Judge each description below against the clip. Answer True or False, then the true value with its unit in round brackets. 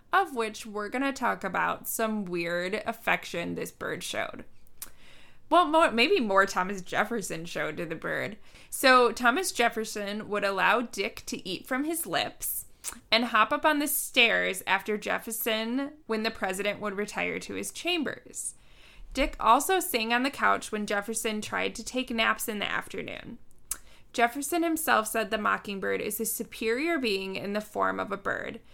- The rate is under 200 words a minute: True (165 wpm)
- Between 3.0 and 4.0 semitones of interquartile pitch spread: True (3.7 semitones)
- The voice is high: True (225 Hz)